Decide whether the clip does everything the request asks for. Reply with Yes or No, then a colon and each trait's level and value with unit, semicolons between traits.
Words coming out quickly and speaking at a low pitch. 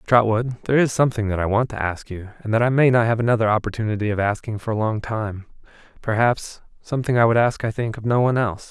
Yes: fast, 235 wpm; low, 110 Hz